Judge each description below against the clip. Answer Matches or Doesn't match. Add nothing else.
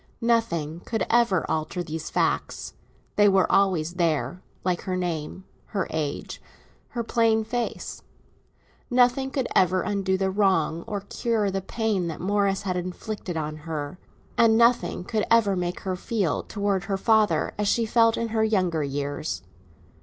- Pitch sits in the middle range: Doesn't match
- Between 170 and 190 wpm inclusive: Doesn't match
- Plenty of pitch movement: Doesn't match